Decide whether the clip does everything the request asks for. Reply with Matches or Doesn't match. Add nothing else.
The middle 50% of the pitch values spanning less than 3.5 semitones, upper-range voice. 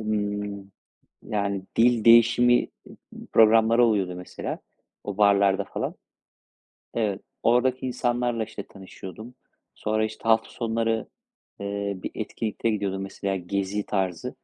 Doesn't match